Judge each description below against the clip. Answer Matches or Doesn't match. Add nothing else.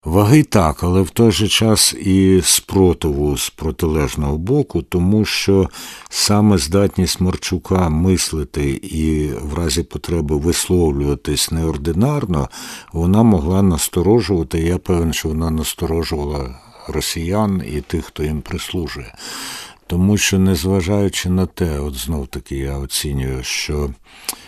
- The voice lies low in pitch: Matches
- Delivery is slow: Matches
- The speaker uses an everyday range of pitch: Matches